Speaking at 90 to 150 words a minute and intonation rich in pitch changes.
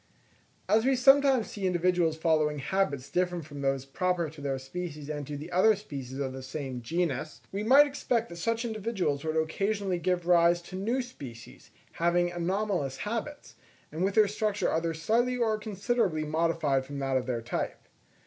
No: average, 175 wpm; wide, 6.5 semitones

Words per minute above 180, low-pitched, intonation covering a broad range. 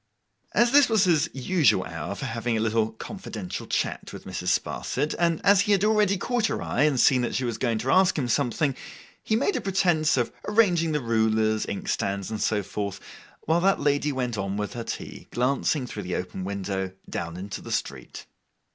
Yes: average, 200 wpm; low, 125 Hz; wide, 8.4 semitones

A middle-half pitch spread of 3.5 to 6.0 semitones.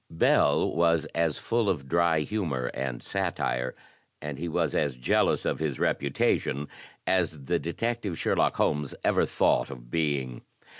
Yes: average, 4.2 semitones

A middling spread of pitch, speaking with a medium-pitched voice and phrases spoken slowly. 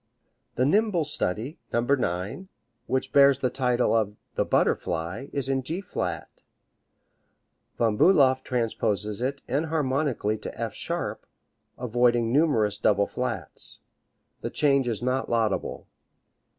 No: average, 4.2 semitones; low, 125 Hz; slow, 120 wpm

